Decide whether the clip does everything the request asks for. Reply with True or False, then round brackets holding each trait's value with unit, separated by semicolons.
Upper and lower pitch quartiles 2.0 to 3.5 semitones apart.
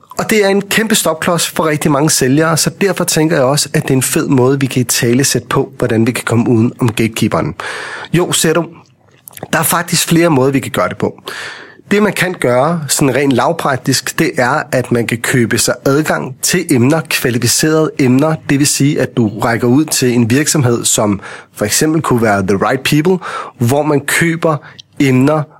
False (4.4 semitones)